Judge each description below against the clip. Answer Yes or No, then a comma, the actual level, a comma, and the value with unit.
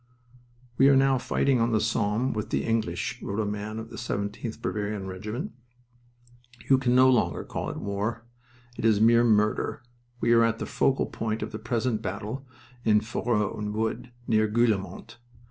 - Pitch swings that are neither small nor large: No, narrow, 2.2 semitones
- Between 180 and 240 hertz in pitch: No, low, 110 Hz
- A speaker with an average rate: Yes, average, 170 wpm